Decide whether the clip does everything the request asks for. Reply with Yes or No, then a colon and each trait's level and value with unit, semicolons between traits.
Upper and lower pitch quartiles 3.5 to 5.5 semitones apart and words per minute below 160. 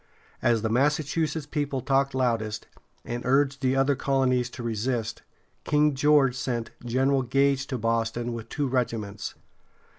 No: average, 2.9 semitones; average, 140 wpm